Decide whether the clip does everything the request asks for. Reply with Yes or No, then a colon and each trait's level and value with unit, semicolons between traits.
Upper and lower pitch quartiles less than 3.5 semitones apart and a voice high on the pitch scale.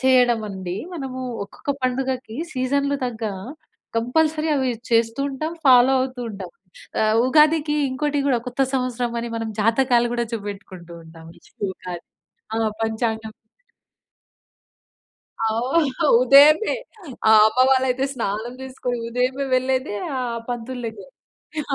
Yes: average, 3.0 semitones; very high, 250 Hz